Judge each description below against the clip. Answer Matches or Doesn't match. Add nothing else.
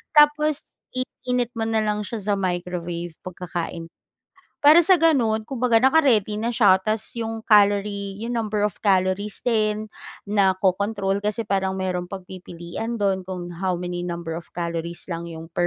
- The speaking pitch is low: Doesn't match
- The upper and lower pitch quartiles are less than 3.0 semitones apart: Doesn't match